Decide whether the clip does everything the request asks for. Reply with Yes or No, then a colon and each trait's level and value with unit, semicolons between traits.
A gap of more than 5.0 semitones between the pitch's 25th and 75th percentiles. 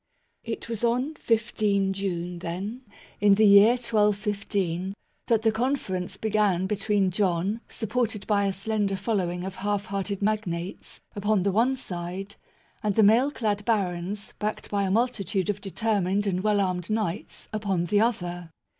No: narrow, 2.4 semitones